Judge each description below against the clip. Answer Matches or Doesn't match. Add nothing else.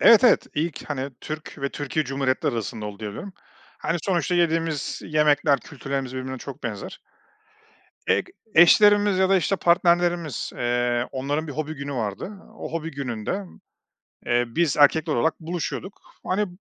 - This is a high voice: Doesn't match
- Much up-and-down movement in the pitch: Doesn't match